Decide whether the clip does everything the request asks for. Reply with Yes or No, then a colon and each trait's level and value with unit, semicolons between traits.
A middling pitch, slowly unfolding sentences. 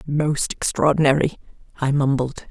Yes: medium, 145 Hz; slow, 95 wpm